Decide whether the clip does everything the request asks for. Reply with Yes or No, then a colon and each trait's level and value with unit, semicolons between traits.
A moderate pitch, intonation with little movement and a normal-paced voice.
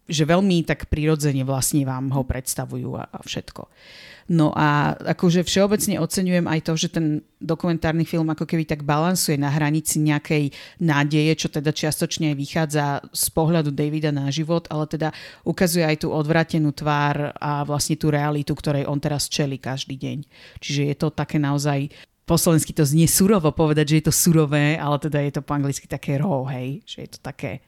No: medium, 155 Hz; narrow, 2.0 semitones; fast, 180 wpm